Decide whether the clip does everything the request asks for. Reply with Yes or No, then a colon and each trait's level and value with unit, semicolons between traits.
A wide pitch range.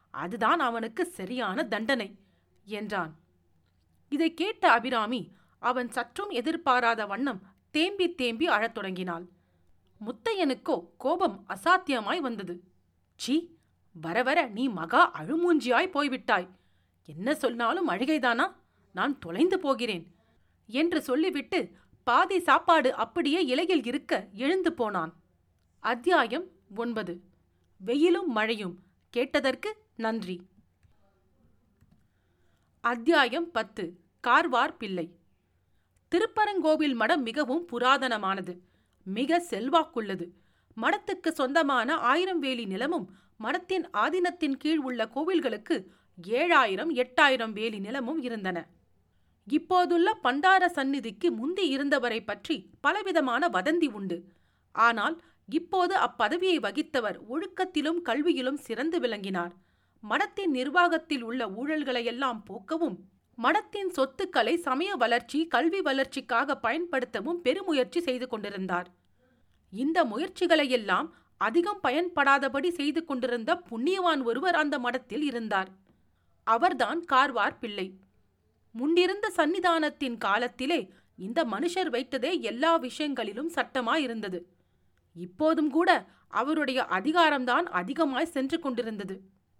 Yes: wide, 7.9 semitones